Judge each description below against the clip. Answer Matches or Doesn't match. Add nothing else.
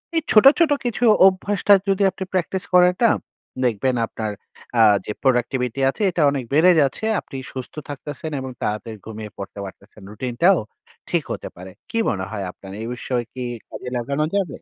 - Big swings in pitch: Matches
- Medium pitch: Doesn't match